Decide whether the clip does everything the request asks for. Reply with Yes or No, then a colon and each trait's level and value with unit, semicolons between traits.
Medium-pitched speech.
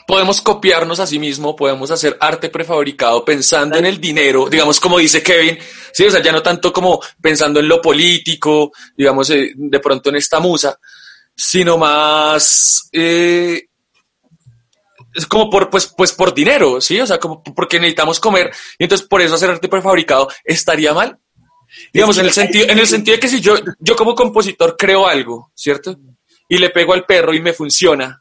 Yes: medium, 165 Hz